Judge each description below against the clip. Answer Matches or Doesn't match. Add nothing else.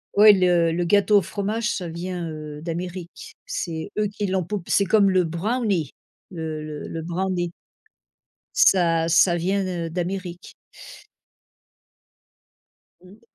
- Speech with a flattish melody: Doesn't match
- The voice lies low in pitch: Doesn't match